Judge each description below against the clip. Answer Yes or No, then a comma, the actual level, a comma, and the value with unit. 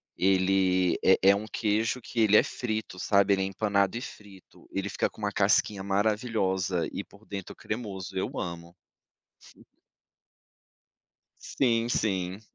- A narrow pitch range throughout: Yes, narrow, 2.3 semitones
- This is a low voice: Yes, low, 100 Hz